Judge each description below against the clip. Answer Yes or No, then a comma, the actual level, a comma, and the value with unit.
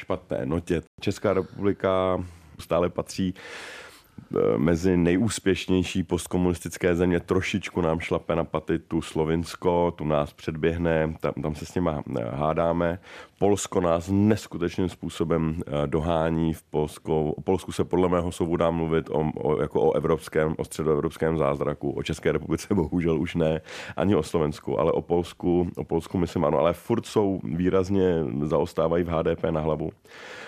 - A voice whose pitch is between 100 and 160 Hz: No, very low, 85 Hz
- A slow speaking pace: No, average, 145 wpm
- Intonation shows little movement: Yes, narrow, 2.1 semitones